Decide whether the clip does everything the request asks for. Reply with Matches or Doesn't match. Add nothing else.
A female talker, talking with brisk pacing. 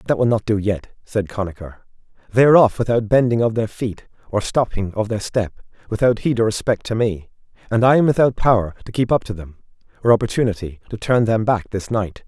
Doesn't match